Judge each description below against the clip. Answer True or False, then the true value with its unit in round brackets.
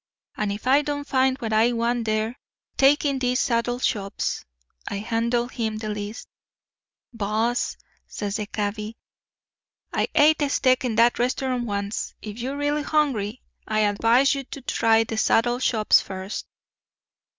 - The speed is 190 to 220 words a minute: False (150 wpm)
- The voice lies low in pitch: False (230 Hz)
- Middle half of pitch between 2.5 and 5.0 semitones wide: True (3.2 semitones)